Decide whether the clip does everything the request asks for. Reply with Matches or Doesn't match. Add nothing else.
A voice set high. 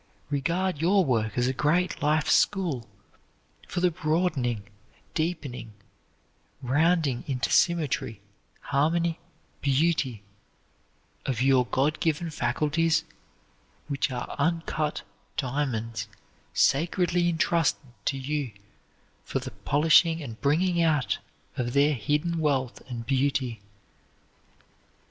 Doesn't match